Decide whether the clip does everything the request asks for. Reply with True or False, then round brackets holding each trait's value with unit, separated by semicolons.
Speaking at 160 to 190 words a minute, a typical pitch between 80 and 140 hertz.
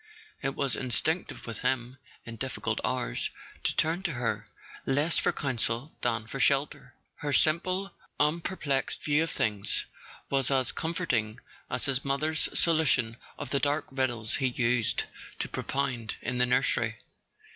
False (150 wpm; 135 Hz)